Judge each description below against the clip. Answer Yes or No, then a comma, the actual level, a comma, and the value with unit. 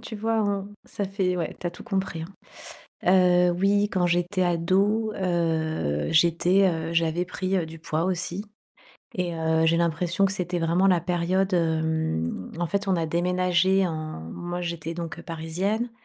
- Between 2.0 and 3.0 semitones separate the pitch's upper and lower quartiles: Yes, narrow, 2.6 semitones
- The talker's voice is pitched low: No, medium, 175 Hz